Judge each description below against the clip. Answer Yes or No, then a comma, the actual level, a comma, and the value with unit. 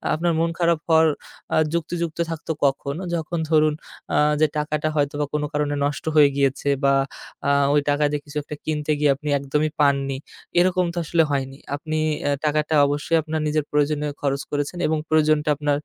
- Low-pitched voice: No, medium, 150 Hz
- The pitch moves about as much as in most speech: No, narrow, 1.5 semitones